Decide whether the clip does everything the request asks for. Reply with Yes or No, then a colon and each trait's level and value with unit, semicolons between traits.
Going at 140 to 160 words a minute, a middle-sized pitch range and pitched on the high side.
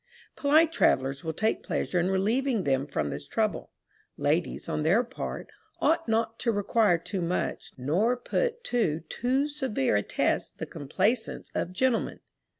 No: average, 150 wpm; wide, 7.8 semitones; high, 215 Hz